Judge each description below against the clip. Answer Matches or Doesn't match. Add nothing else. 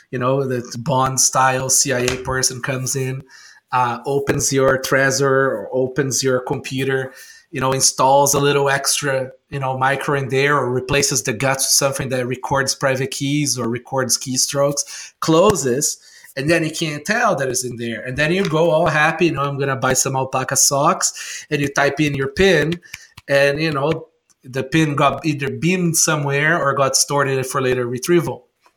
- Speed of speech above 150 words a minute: Matches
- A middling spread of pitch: Doesn't match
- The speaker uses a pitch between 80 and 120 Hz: Doesn't match